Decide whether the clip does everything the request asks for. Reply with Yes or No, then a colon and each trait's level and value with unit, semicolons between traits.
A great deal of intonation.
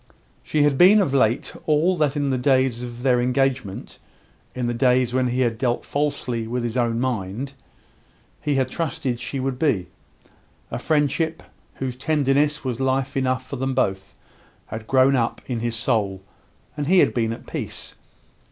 No: average, 2.8 semitones